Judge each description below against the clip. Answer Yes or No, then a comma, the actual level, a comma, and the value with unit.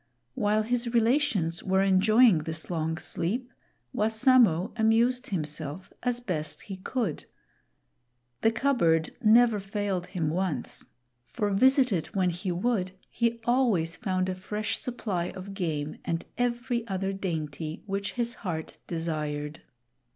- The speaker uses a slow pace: Yes, slow, 130 wpm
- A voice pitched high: Yes, high, 195 Hz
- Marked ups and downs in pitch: Yes, wide, 5.8 semitones